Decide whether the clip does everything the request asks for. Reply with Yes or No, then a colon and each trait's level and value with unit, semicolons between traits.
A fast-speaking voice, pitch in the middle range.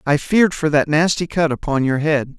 Yes: fast, 225 wpm; medium, 150 Hz